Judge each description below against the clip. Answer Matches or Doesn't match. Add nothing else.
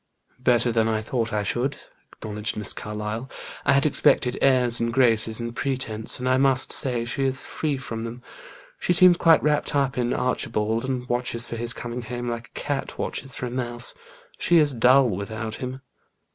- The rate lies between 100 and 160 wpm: Doesn't match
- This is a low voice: Matches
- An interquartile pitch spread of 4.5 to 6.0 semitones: Doesn't match